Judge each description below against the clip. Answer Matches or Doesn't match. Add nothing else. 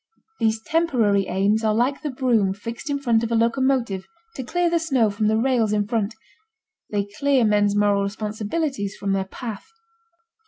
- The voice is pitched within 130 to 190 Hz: Doesn't match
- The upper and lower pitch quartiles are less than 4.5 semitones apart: Matches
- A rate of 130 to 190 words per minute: Matches